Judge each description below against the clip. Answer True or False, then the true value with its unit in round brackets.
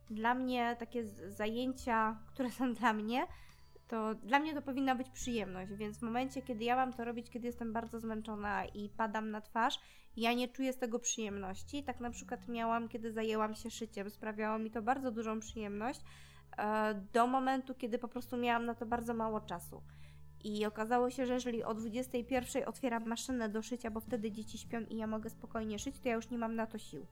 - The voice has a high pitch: True (230 Hz)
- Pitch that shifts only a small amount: True (2.1 semitones)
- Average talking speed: False (200 wpm)